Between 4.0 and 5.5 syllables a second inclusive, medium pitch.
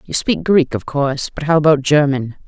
Yes: 5.3 syllables/s; medium, 145 Hz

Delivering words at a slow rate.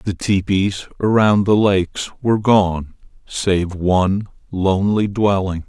Yes: slow, 115 wpm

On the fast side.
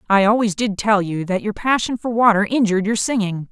Yes: fast, 220 wpm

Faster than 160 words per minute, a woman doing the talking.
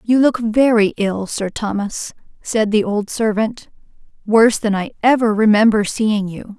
No: average, 155 wpm; female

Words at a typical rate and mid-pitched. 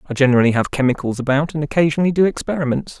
Yes: average, 180 wpm; medium, 145 Hz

